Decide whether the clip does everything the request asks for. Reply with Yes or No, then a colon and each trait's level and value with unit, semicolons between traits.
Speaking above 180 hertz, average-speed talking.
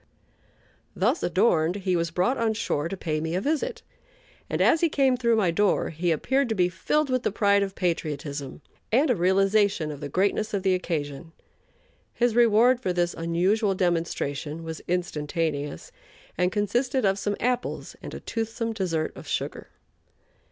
Yes: high, 190 Hz; average, 165 wpm